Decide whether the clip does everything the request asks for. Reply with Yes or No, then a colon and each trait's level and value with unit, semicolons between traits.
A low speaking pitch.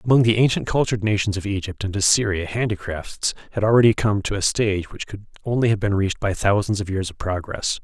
Yes: low, 105 Hz